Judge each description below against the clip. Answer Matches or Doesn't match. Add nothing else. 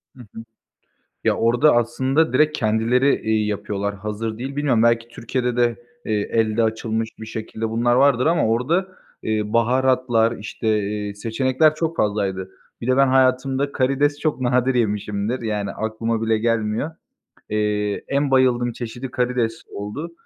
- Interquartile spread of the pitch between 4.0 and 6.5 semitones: Doesn't match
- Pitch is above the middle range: Doesn't match